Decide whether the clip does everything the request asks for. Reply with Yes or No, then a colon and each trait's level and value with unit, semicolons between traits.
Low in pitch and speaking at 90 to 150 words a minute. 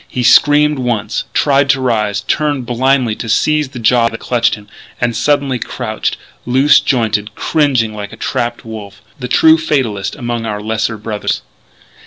No: low, 120 Hz; average, 160 wpm